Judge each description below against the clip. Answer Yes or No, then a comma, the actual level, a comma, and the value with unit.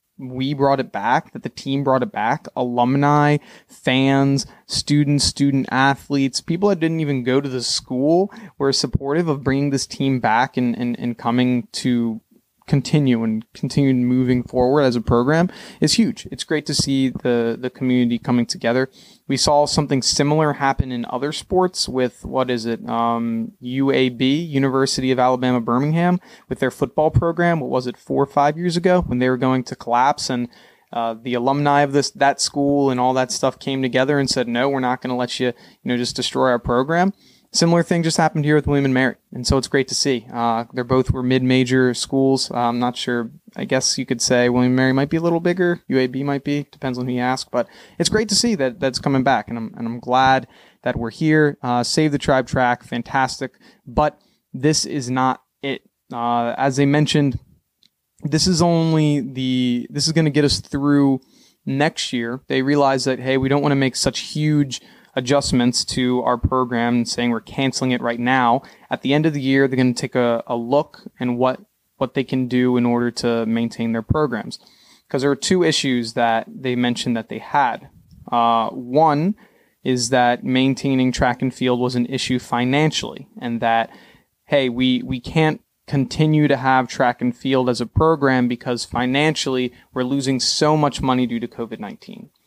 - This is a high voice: No, low, 130 Hz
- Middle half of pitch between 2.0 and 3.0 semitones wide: Yes, average, 2.7 semitones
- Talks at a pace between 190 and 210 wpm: Yes, average, 200 wpm